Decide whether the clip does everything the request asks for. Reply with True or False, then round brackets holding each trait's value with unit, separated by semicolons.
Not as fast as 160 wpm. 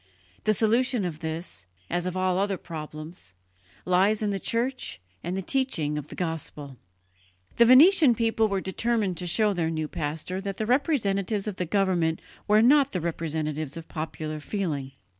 False (165 wpm)